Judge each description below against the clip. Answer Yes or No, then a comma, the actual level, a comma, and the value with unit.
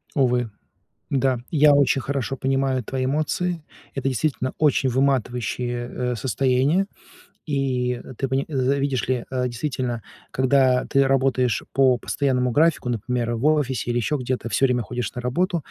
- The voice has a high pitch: No, low, 130 Hz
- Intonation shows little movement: Yes, narrow, 1.8 semitones